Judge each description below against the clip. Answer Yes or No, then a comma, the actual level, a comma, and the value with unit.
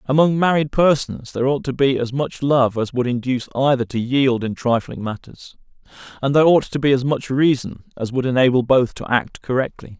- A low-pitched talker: Yes, low, 130 Hz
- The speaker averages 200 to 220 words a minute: Yes, fast, 205 wpm